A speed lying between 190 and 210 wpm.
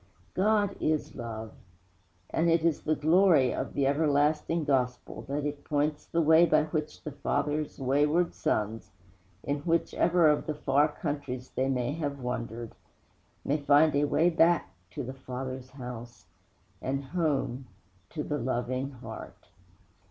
No: average, 145 wpm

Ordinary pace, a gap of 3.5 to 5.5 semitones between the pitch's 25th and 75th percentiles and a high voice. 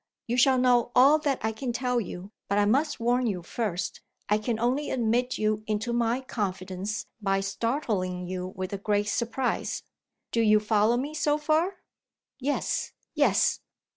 Yes: average, 165 wpm; average, 3.8 semitones; high, 230 Hz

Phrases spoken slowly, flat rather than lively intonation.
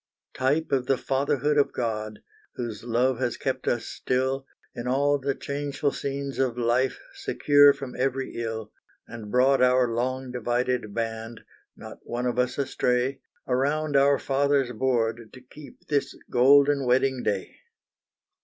No: average, 145 wpm; narrow, 2.3 semitones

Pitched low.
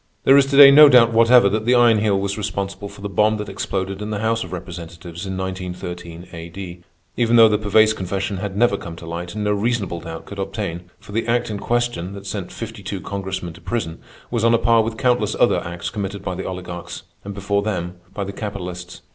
Yes: low, 100 Hz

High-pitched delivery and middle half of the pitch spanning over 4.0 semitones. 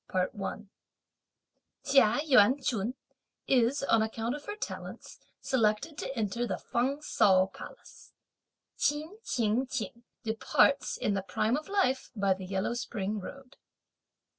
Yes: high, 240 Hz; average, 4.6 semitones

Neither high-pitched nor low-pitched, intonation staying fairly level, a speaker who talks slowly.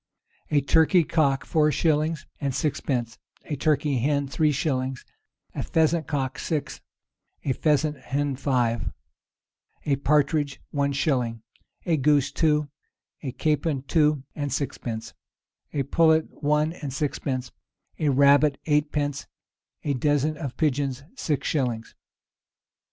Yes: medium, 145 Hz; narrow, 2.3 semitones; slow, 120 wpm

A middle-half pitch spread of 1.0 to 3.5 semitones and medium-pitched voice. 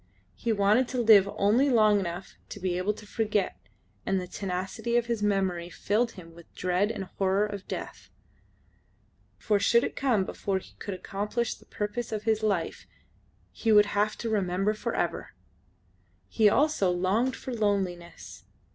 No: average, 2.7 semitones; high, 205 Hz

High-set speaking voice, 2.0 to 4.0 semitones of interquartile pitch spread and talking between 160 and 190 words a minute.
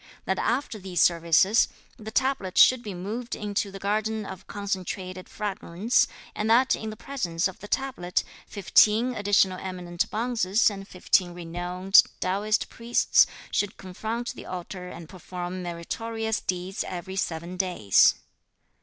No: high, 195 Hz; average, 3.2 semitones; slow, 135 wpm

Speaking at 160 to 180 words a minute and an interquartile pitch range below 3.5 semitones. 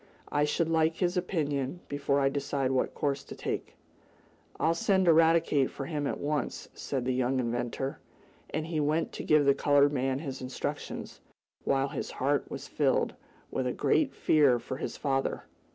Yes: average, 170 wpm; average, 2.8 semitones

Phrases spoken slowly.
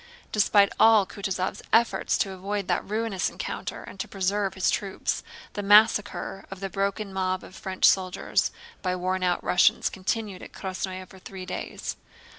No: average, 160 wpm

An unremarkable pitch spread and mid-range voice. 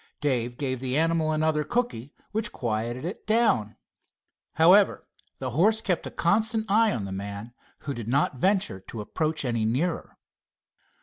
No: wide, 8.2 semitones; medium, 150 Hz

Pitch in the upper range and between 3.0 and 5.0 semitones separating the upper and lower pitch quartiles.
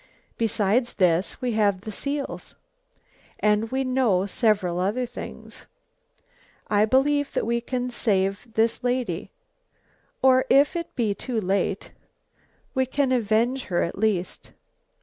Yes: high, 225 Hz; average, 4.4 semitones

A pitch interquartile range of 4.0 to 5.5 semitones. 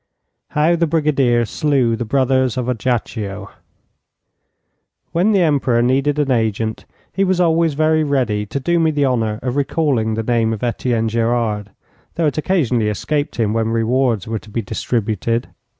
Yes: average, 4.9 semitones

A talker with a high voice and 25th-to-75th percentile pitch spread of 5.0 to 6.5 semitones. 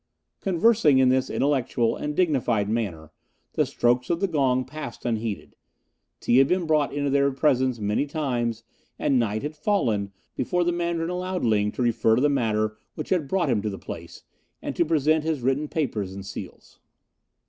No: low, 135 Hz; wide, 5.4 semitones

